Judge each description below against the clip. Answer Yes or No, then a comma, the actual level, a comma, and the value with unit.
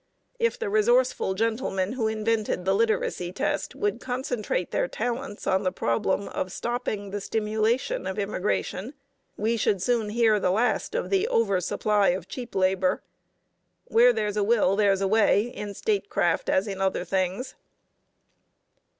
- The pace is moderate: Yes, average, 150 wpm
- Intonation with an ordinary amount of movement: Yes, average, 3.9 semitones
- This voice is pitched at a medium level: No, high, 215 Hz